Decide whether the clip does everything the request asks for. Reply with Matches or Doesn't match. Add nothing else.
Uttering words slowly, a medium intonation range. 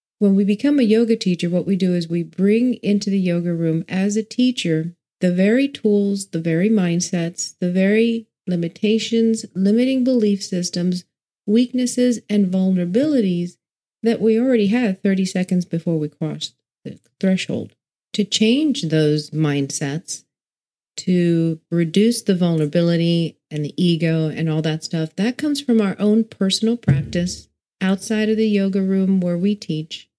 Doesn't match